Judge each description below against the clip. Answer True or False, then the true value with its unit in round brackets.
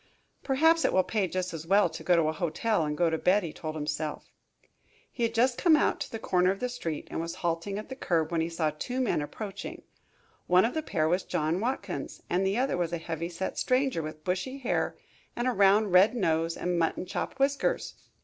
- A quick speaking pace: True (225 wpm)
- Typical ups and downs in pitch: False (5.8 semitones)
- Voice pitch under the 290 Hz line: True (185 Hz)